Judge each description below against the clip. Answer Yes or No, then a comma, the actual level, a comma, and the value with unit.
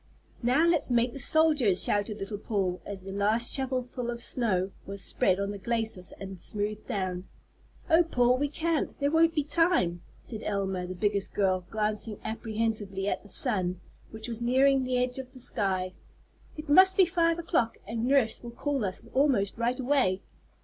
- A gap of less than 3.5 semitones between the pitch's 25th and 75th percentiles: No, average, 5.3 semitones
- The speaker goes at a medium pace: Yes, average, 180 wpm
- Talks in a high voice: Yes, high, 230 Hz